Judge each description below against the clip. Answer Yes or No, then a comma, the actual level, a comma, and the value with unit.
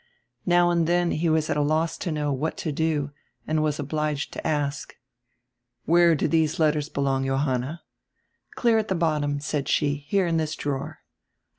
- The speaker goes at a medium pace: Yes, average, 175 wpm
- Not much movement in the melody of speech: Yes, narrow, 2.3 semitones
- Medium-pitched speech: Yes, medium, 155 Hz